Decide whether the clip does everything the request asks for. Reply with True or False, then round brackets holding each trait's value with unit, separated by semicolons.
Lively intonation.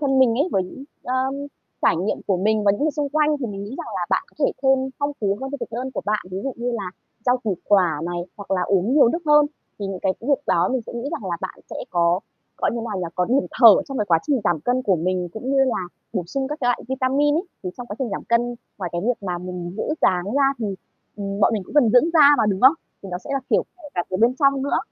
True (5.9 semitones)